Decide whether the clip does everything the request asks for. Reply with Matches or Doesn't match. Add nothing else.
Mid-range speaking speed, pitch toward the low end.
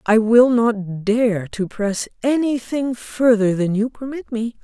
Doesn't match